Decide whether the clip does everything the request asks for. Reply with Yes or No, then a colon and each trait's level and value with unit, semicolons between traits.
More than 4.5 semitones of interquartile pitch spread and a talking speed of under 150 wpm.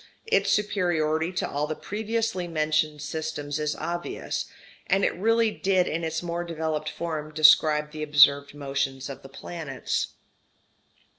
No: average, 2.8 semitones; average, 140 wpm